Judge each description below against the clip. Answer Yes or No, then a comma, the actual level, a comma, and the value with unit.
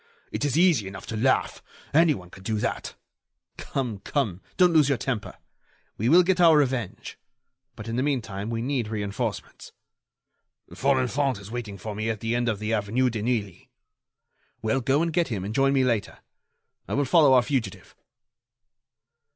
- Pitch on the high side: No, low, 120 Hz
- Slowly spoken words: No, average, 170 wpm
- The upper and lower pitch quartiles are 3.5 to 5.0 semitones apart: Yes, average, 4.5 semitones